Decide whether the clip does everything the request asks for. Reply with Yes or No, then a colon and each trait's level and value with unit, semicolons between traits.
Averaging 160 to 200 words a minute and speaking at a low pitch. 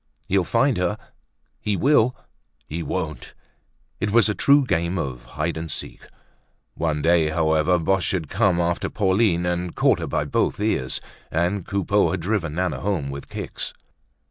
No: average, 150 wpm; very low, 90 Hz